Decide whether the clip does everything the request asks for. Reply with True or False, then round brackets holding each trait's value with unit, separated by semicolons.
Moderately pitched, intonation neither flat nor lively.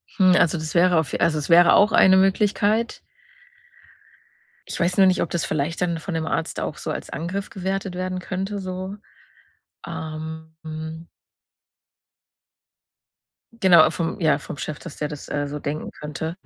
True (170 Hz; 3.0 semitones)